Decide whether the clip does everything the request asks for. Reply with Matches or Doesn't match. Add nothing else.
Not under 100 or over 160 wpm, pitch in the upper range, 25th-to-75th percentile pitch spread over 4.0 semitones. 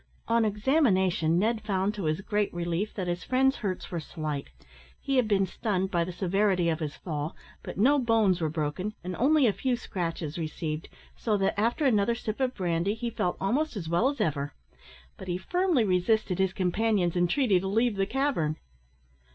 Doesn't match